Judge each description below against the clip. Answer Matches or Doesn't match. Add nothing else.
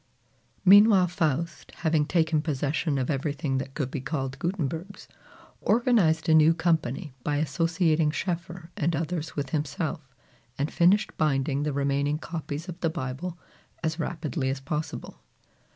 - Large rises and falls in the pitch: Doesn't match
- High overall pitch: Doesn't match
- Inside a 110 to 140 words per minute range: Matches